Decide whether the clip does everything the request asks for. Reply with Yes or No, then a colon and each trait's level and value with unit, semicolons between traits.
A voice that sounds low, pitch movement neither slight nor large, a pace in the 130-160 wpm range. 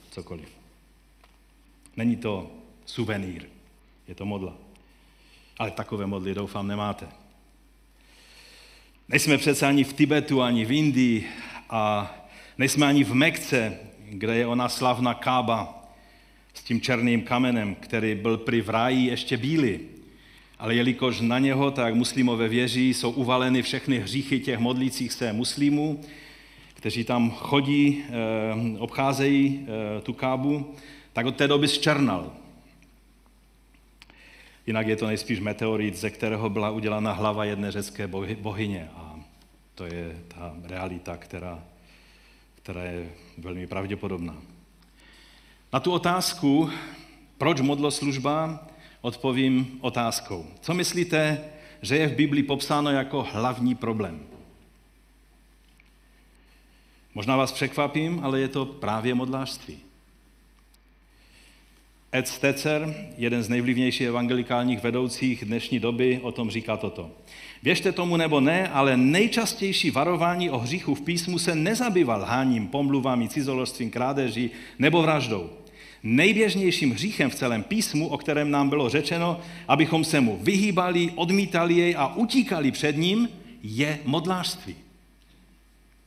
No: low, 125 Hz; average, 5.0 semitones; average, 120 wpm